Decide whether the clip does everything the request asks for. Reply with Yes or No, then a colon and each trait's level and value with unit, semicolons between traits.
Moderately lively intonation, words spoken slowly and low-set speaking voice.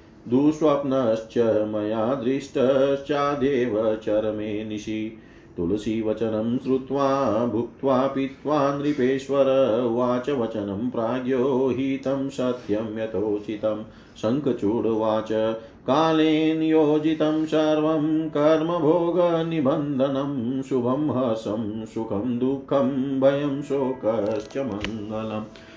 Yes: average, 4.3 semitones; slow, 65 wpm; low, 130 Hz